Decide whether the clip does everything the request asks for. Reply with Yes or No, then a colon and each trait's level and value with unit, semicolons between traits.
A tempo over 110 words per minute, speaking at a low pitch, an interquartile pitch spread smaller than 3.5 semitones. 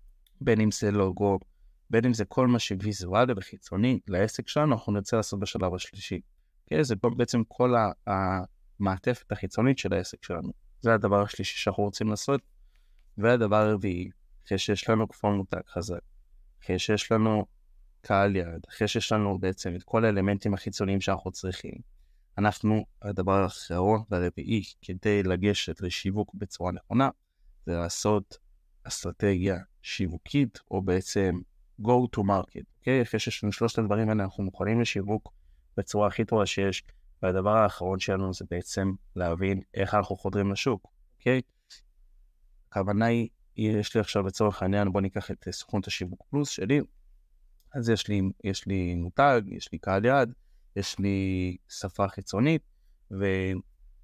Yes: average, 145 wpm; low, 100 Hz; average, 2.8 semitones